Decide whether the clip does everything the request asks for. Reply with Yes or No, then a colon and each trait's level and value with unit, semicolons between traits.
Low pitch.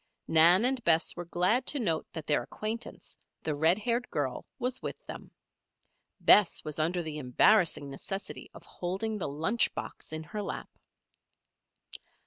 No: medium, 175 Hz